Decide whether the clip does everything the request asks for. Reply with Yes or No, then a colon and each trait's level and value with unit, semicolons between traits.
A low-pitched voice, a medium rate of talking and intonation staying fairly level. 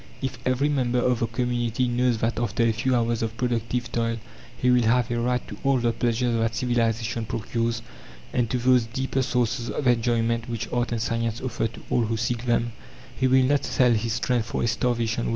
No: low, 120 Hz; fast, 210 wpm; narrow, 1.4 semitones